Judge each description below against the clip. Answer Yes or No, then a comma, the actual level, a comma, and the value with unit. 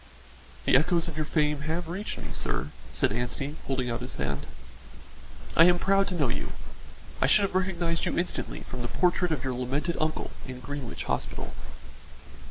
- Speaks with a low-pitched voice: No, medium, 155 Hz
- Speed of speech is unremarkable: Yes, average, 175 wpm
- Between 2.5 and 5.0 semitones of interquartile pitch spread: No, wide, 5.4 semitones